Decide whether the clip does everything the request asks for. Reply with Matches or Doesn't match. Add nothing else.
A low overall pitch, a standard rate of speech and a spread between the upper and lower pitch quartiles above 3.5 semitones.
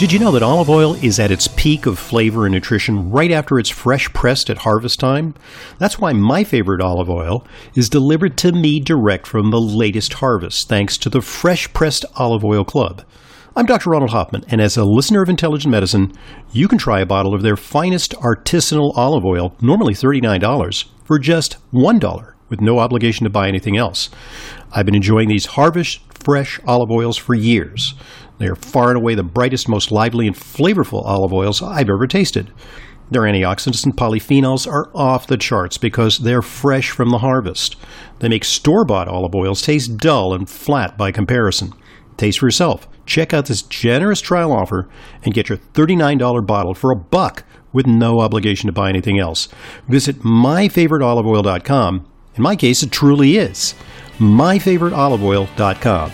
Matches